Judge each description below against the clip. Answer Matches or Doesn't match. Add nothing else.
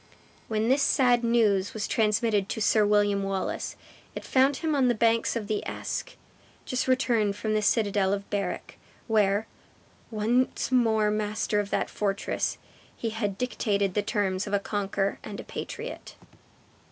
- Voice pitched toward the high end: Matches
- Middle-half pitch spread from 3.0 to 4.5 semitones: Doesn't match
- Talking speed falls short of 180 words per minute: Matches